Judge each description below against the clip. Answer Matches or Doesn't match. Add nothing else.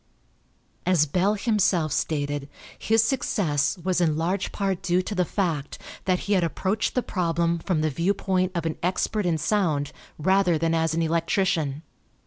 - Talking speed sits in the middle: Matches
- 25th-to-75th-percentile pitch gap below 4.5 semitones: Matches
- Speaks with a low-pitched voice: Doesn't match